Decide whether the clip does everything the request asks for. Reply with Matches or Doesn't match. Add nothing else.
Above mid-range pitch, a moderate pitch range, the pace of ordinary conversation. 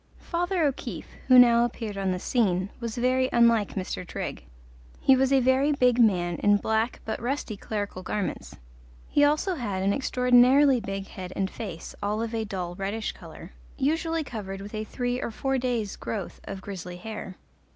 Matches